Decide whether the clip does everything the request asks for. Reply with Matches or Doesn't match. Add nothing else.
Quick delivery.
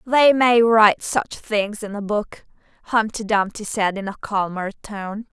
Doesn't match